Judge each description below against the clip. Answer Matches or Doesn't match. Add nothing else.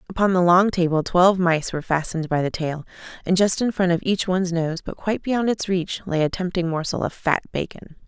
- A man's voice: Doesn't match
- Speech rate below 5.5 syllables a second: Doesn't match